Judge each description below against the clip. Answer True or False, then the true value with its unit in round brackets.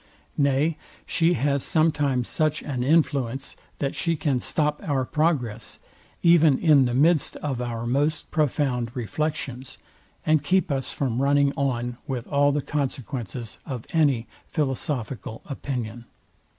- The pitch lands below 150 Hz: True (140 Hz)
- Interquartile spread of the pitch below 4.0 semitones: True (3.4 semitones)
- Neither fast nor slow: False (130 wpm)